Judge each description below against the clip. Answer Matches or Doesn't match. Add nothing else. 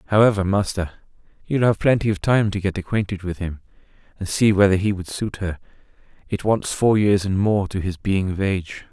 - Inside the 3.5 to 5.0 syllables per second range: Doesn't match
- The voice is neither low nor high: Doesn't match